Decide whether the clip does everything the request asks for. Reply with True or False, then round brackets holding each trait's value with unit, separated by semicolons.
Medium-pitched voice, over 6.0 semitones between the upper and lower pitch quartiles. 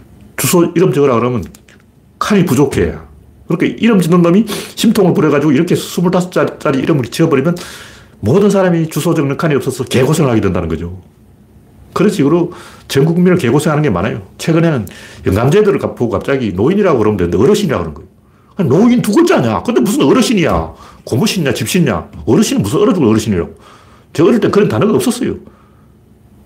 True (150 Hz; 8.7 semitones)